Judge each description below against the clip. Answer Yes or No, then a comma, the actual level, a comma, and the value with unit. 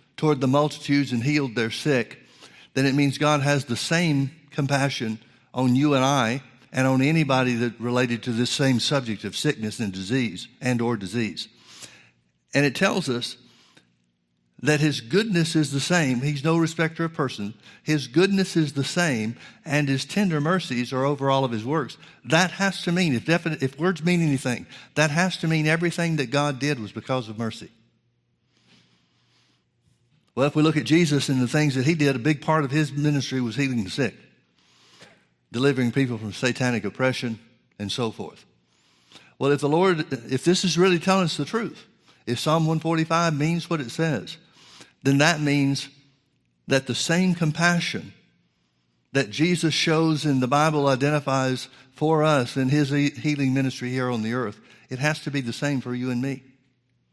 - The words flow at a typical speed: Yes, average, 180 wpm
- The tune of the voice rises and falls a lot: No, average, 4.2 semitones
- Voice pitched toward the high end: No, medium, 140 Hz